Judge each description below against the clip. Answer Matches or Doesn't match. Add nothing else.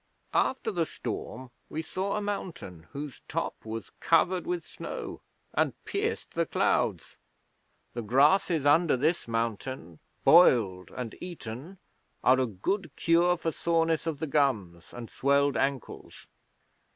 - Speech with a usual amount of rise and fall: Doesn't match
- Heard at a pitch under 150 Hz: Matches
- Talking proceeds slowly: Matches